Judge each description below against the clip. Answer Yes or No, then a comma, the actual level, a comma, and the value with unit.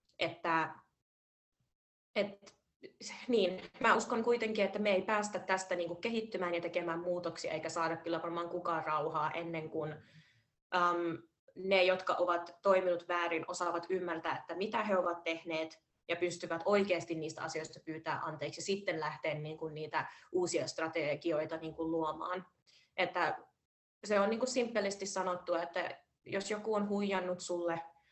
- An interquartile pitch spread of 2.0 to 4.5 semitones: Yes, average, 2.7 semitones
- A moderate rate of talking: Yes, average, 140 wpm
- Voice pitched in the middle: Yes, medium, 175 Hz